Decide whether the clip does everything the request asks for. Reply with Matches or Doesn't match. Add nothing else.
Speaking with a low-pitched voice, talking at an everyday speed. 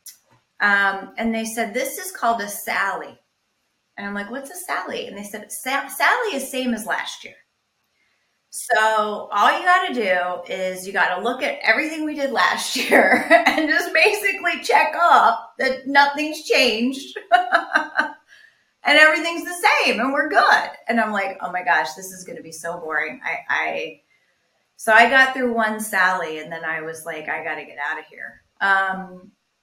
Doesn't match